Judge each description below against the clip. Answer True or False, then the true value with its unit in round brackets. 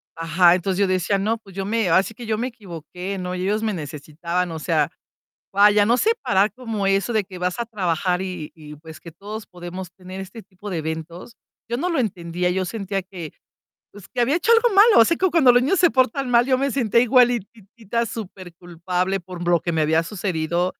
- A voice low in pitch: False (195 Hz)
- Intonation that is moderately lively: True (4.6 semitones)